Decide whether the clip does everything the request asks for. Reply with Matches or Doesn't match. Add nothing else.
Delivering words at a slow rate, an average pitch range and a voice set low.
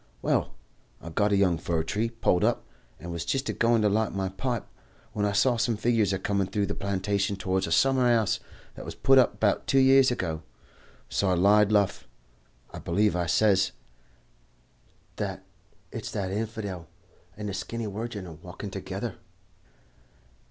Doesn't match